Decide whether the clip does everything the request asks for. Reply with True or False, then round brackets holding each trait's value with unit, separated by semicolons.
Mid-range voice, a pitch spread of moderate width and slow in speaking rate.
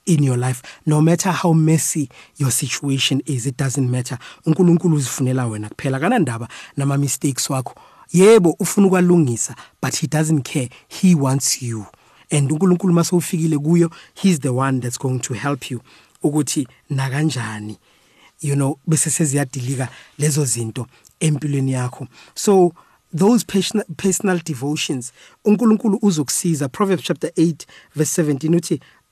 True (150 Hz; 4.3 semitones; 130 wpm)